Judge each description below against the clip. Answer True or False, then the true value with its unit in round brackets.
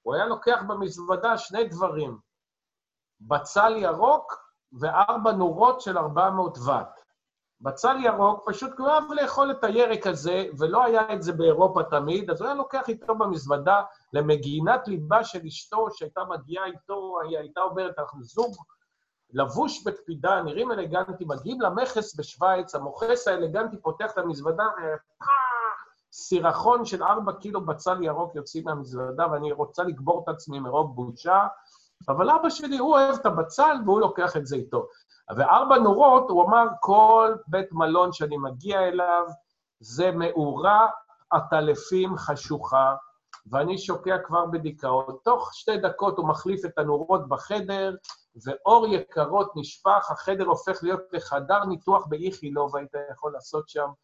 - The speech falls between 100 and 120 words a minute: False (140 wpm)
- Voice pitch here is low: False (185 Hz)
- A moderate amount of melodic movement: False (6.0 semitones)